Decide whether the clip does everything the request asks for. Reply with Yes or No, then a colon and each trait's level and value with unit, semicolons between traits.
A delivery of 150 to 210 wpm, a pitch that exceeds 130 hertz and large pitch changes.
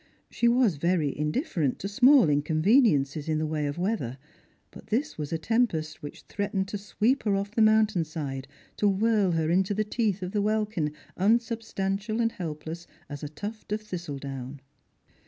Yes: average, 170 wpm; high, 190 Hz; wide, 5.9 semitones